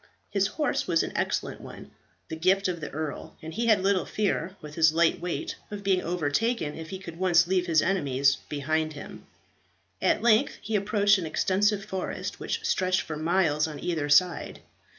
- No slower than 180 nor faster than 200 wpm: Yes, average, 185 wpm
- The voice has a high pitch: No, medium, 180 Hz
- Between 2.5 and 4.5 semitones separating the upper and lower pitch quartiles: Yes, average, 3.8 semitones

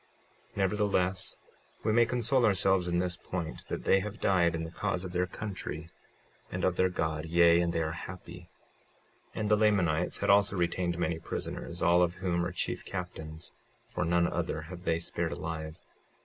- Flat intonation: Yes, narrow, 2.3 semitones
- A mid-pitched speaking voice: No, very low, 90 Hz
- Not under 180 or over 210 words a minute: Yes, average, 185 wpm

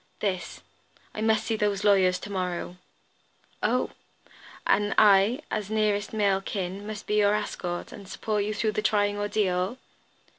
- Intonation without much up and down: Yes, narrow, 1.7 semitones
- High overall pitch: Yes, high, 205 Hz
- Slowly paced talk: No, average, 150 wpm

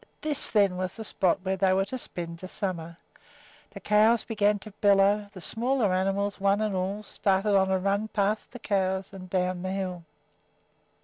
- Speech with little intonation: Yes, narrow, 2.0 semitones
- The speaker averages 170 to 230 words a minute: Yes, average, 185 wpm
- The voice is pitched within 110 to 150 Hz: No, high, 195 Hz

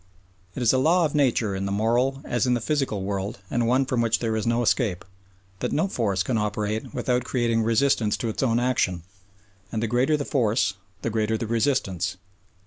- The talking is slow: No, fast, 205 wpm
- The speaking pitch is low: Yes, low, 115 Hz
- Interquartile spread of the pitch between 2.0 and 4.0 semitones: Yes, average, 3.1 semitones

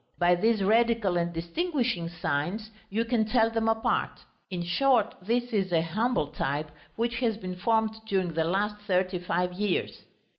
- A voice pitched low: No, high, 205 Hz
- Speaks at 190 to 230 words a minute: No, average, 160 wpm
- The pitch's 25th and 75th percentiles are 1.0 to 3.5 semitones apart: No, average, 4.5 semitones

